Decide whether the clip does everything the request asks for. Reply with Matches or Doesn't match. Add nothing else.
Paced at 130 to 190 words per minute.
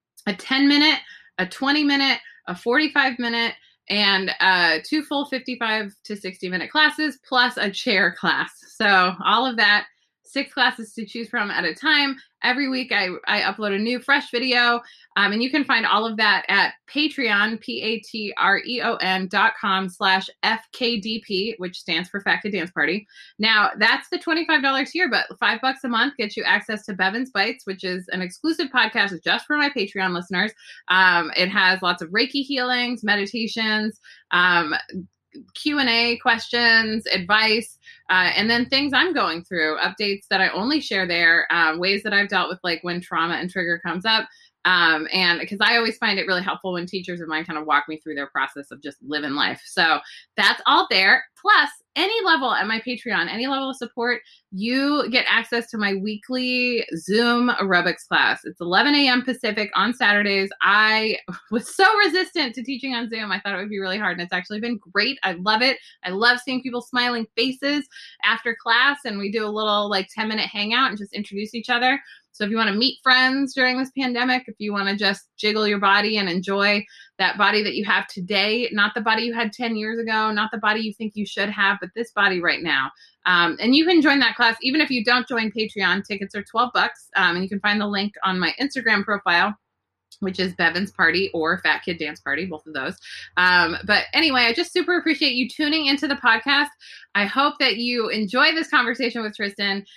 Doesn't match